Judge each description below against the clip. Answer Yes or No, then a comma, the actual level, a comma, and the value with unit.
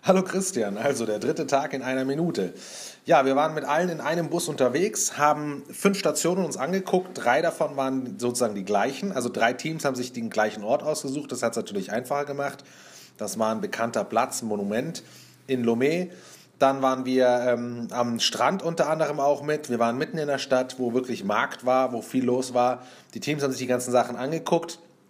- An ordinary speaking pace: No, fast, 205 wpm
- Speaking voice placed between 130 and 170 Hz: Yes, low, 135 Hz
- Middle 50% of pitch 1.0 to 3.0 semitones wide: No, average, 4.3 semitones